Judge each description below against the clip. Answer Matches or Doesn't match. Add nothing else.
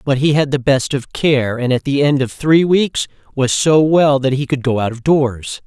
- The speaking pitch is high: Doesn't match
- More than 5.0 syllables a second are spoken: Doesn't match